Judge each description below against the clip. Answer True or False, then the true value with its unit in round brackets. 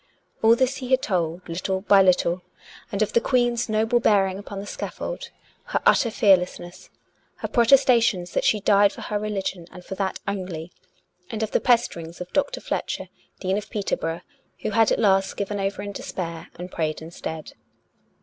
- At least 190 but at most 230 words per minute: False (180 wpm)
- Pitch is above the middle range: True (200 Hz)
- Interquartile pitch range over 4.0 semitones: False (3.7 semitones)